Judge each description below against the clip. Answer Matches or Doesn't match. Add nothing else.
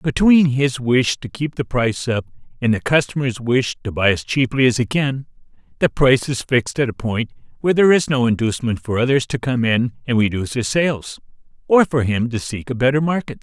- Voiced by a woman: Doesn't match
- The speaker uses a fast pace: Matches